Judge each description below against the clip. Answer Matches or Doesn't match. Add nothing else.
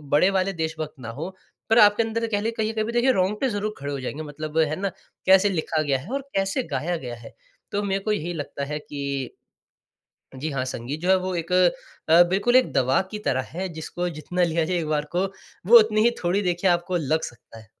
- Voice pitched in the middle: Matches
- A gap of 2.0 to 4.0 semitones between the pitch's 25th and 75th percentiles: Doesn't match